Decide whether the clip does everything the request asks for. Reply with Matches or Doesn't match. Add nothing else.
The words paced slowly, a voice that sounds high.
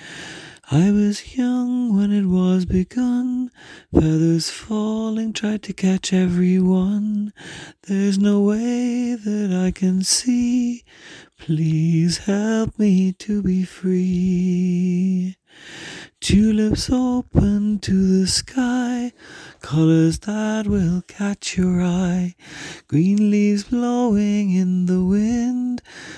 Matches